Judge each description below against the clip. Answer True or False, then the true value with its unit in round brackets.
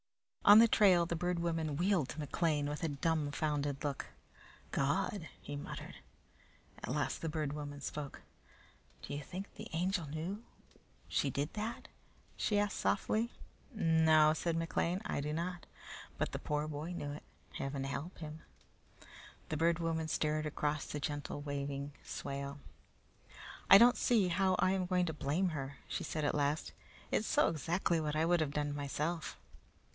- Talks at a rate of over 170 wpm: False (160 wpm)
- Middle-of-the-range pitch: True (155 Hz)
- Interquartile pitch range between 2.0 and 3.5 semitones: True (3.2 semitones)